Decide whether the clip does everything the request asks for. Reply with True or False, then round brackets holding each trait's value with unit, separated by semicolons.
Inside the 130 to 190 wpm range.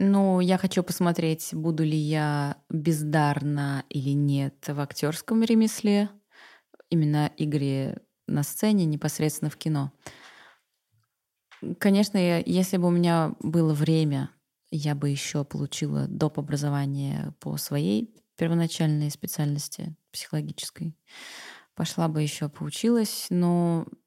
False (110 wpm)